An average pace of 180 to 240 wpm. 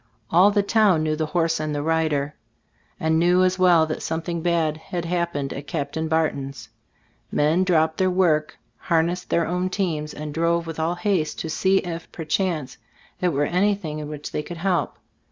Yes: average, 190 wpm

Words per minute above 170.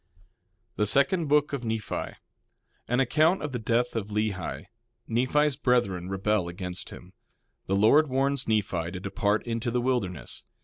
No: average, 145 wpm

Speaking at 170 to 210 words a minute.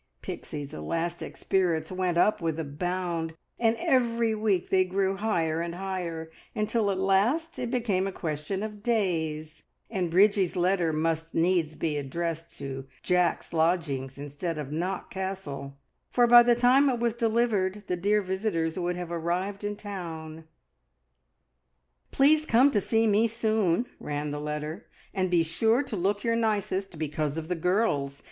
No: average, 155 wpm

